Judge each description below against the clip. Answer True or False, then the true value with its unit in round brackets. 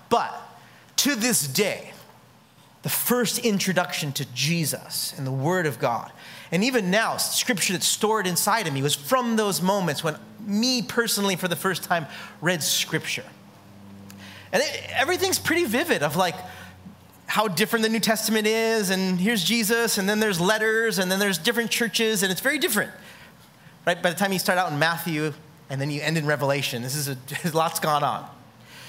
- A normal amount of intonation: False (6.3 semitones)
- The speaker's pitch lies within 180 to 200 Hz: True (185 Hz)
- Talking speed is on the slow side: False (180 wpm)